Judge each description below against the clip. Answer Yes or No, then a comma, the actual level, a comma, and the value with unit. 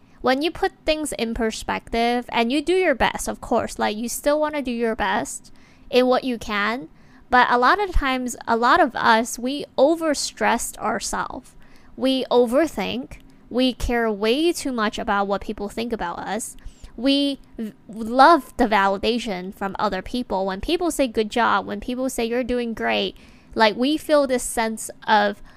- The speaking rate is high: No, average, 175 wpm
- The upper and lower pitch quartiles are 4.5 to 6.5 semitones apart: No, average, 3.6 semitones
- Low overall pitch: No, high, 245 Hz